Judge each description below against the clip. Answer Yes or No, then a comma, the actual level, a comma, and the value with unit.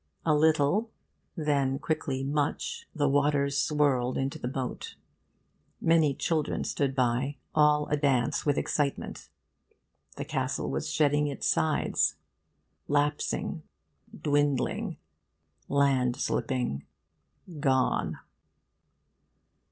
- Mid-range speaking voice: Yes, medium, 145 Hz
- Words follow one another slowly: Yes, slow, 90 wpm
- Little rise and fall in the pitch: Yes, narrow, 1.9 semitones